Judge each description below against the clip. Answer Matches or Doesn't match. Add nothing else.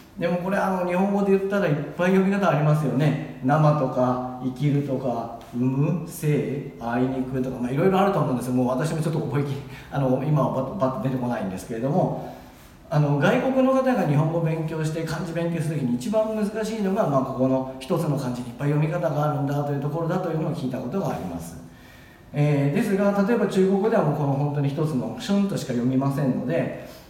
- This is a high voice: Doesn't match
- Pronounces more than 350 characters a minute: Matches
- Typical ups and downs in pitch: Matches